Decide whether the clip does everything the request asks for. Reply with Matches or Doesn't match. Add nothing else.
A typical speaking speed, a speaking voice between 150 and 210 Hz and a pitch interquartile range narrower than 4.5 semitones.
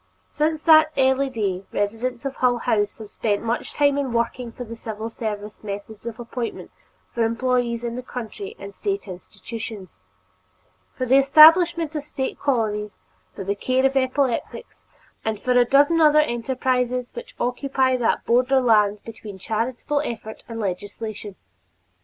Doesn't match